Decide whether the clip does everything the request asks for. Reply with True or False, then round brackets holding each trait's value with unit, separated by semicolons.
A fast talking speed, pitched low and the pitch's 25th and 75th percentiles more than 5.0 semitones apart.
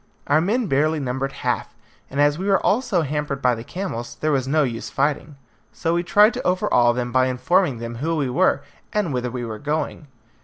False (215 wpm; 145 Hz; 5.4 semitones)